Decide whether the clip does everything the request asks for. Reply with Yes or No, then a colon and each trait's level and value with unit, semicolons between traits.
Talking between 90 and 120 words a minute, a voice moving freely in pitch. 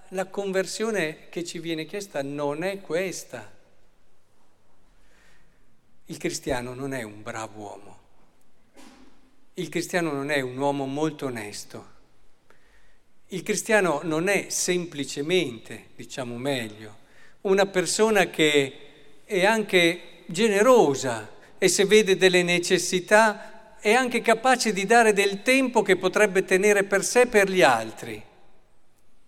Yes: slow, 115 wpm; wide, 6.3 semitones